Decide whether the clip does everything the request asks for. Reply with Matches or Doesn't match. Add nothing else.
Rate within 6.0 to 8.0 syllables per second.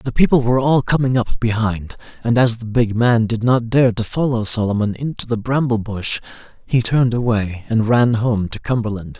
Doesn't match